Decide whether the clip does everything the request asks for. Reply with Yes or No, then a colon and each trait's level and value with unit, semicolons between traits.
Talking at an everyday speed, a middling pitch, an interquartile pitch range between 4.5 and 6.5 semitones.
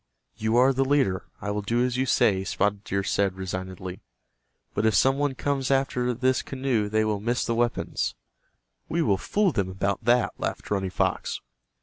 No: average, 185 wpm; low, 110 Hz; average, 4.8 semitones